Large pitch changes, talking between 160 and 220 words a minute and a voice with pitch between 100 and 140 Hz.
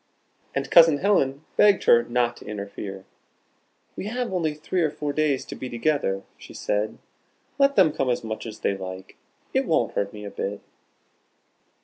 Yes: wide, 7.4 semitones; average, 170 wpm; low, 135 Hz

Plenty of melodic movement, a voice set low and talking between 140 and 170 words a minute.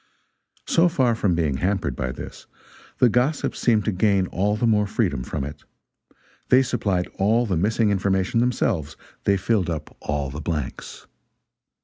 Yes: wide, 5.7 semitones; low, 100 Hz; average, 155 wpm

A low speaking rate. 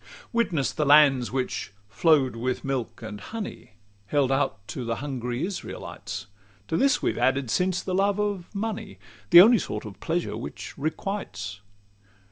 No: average, 160 wpm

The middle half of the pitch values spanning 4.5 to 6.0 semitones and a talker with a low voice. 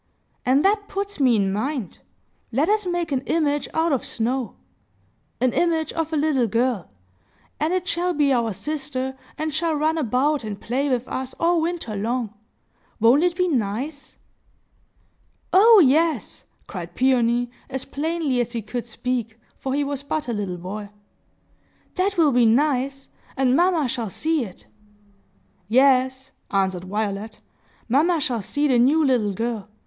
No: average, 5.3 semitones; very high, 265 Hz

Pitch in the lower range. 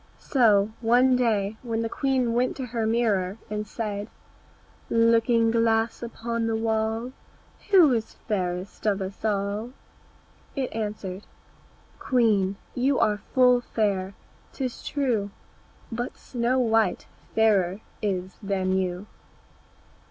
No: high, 225 Hz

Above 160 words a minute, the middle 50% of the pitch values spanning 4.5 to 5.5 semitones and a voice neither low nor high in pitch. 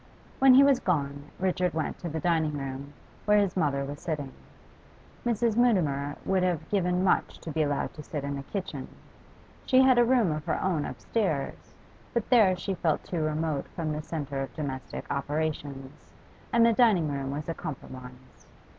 Yes: average, 180 wpm; average, 5.2 semitones; medium, 160 Hz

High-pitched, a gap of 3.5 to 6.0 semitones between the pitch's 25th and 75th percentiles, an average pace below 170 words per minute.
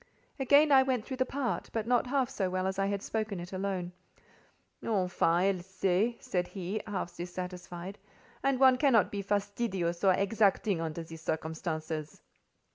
Yes: high, 195 Hz; average, 4.2 semitones; average, 160 wpm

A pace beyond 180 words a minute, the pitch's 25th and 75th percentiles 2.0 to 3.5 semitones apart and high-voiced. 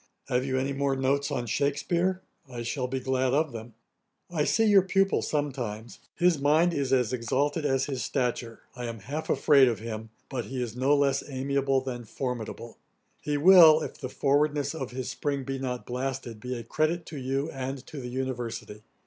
No: average, 190 wpm; average, 2.8 semitones; low, 135 Hz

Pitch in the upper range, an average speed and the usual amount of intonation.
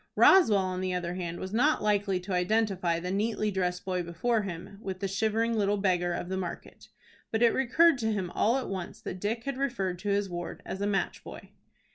No: high, 195 Hz; fast, 215 wpm; average, 3.5 semitones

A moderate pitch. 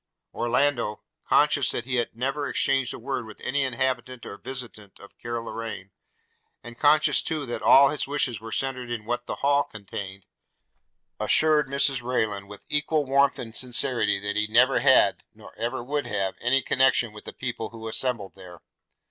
No: low, 120 Hz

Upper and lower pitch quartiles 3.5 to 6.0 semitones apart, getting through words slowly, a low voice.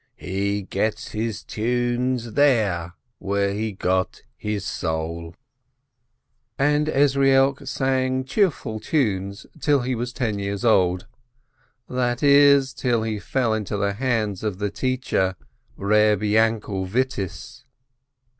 Yes: average, 4.6 semitones; slow, 115 wpm; low, 110 Hz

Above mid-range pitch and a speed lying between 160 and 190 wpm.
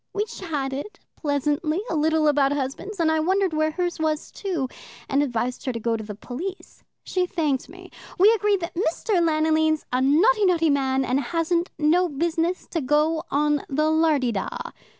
Yes: very high, 315 Hz; average, 175 wpm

